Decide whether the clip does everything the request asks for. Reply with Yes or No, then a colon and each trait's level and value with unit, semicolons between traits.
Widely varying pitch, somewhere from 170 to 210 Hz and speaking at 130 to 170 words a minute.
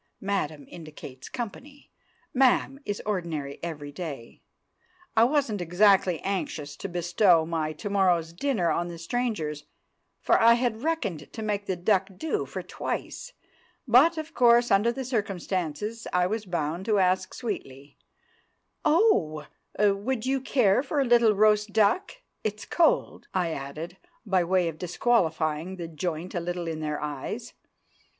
Yes: wide, 5.9 semitones; high, 190 Hz; average, 145 wpm